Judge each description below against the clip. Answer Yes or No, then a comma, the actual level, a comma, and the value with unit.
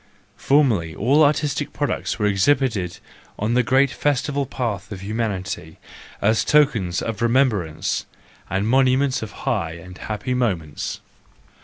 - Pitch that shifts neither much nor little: No, wide, 5.9 semitones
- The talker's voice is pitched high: No, low, 115 Hz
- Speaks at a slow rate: Yes, slow, 125 wpm